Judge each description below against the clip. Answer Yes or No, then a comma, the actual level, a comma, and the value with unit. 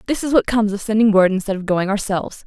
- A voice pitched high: Yes, high, 210 Hz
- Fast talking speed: Yes, fast, 270 wpm